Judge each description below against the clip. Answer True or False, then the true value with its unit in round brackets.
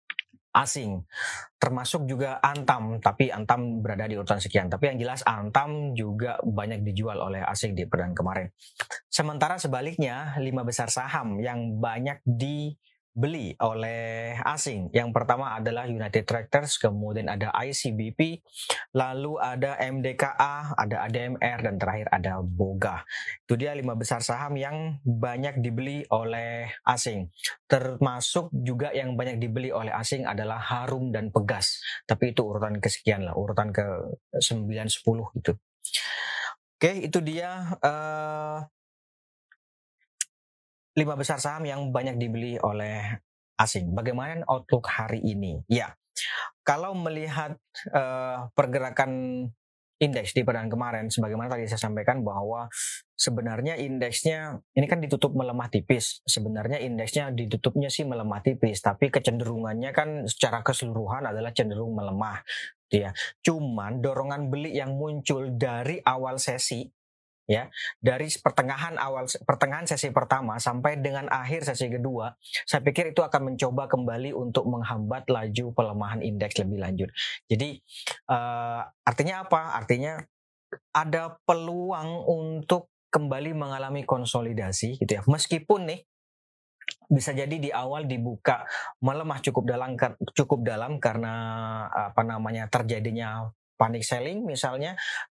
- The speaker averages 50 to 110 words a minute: False (125 wpm)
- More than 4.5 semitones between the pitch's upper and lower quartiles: False (4.2 semitones)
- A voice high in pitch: False (125 Hz)